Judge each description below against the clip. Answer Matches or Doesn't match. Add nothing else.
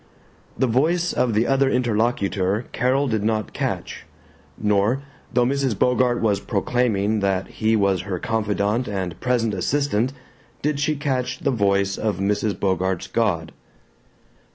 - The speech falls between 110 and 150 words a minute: Matches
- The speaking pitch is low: Matches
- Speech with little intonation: Doesn't match